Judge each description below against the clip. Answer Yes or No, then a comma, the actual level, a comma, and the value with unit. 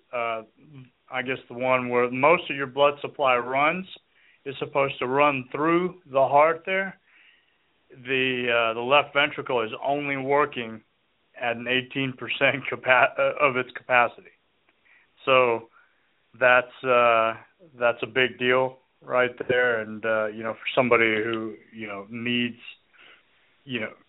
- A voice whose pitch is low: Yes, low, 130 Hz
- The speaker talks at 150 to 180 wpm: No, average, 140 wpm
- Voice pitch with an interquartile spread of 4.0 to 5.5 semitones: No, average, 3.1 semitones